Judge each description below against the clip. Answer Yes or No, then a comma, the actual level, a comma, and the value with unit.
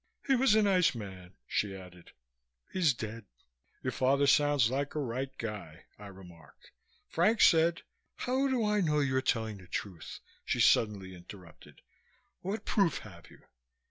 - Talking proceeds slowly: No, average, 155 wpm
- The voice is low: Yes, low, 130 Hz